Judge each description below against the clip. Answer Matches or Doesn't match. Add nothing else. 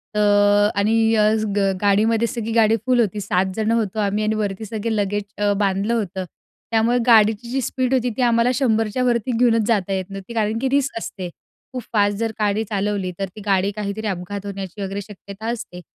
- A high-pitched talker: Matches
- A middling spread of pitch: Doesn't match